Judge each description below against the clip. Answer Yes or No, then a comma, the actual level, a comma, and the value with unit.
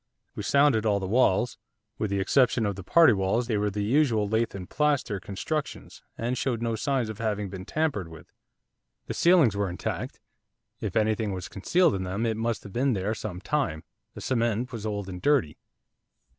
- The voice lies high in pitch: No, low, 110 Hz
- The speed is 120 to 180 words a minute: No, average, 190 wpm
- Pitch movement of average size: Yes, average, 4.2 semitones